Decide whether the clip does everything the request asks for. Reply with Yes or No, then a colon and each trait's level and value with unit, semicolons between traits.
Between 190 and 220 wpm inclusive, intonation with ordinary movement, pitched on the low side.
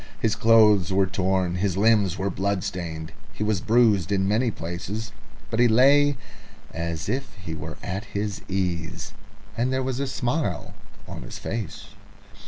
No: average, 160 wpm; average, 3.9 semitones; low, 100 Hz